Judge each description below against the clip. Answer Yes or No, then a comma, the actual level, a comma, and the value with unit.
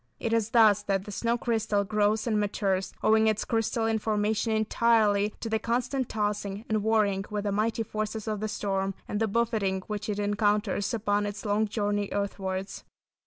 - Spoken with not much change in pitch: Yes, narrow, 1.5 semitones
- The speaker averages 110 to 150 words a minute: No, average, 175 wpm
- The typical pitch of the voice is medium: No, high, 210 Hz